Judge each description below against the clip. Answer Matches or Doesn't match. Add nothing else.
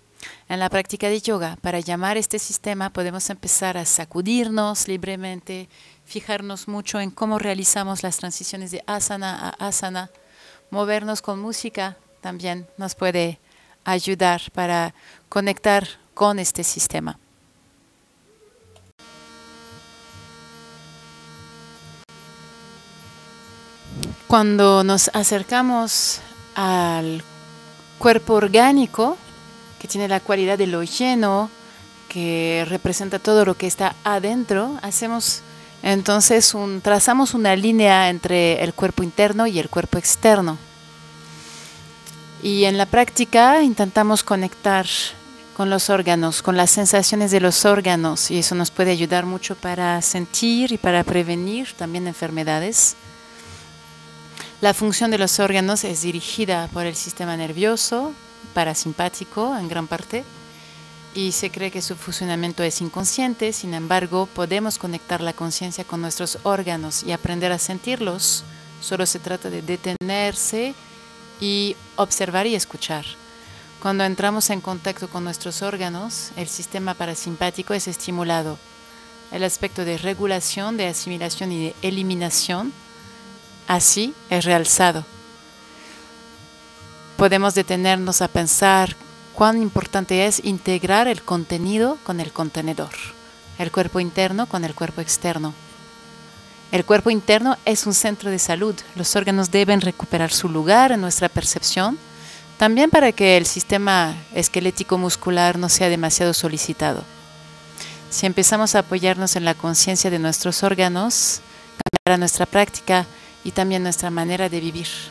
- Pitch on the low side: Doesn't match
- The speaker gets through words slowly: Matches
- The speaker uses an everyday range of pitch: Matches